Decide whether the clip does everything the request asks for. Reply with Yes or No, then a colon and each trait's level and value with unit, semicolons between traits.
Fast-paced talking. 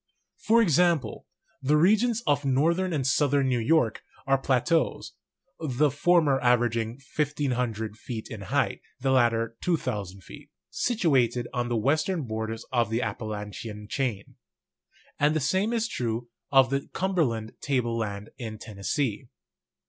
No: average, 140 wpm